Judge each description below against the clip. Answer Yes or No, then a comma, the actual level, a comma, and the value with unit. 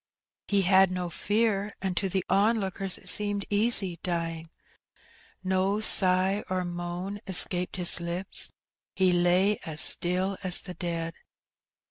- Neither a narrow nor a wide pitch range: No, narrow, 2.0 semitones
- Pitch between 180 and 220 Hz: Yes, medium, 185 Hz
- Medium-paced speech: No, slow, 130 wpm